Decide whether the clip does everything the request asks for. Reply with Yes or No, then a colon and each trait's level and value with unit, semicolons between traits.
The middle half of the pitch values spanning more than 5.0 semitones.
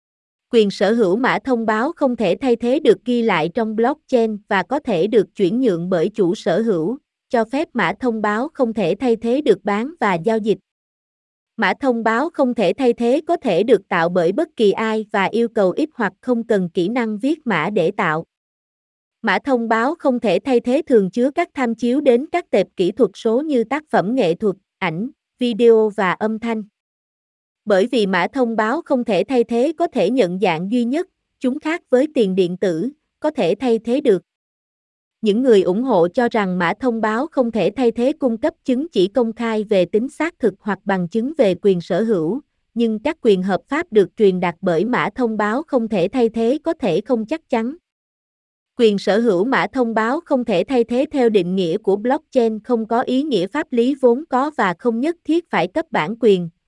No: average, 4.2 semitones